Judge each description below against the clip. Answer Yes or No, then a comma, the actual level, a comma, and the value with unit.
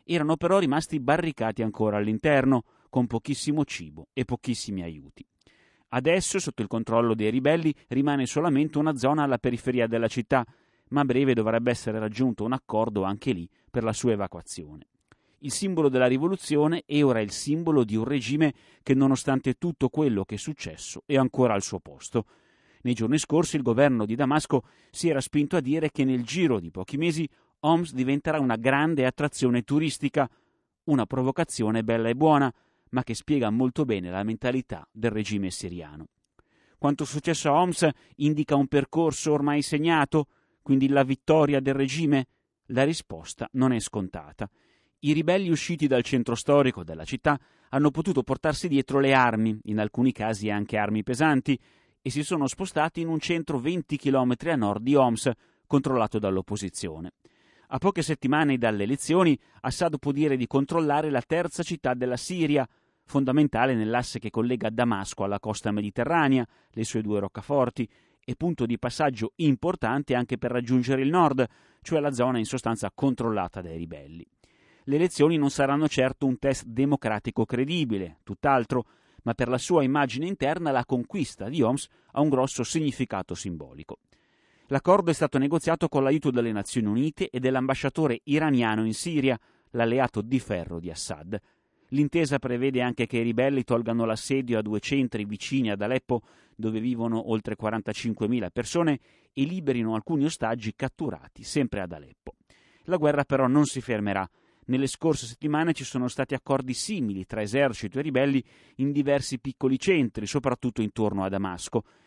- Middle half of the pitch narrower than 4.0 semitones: No, average, 4.6 semitones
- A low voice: Yes, low, 130 Hz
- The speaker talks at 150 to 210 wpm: Yes, average, 160 wpm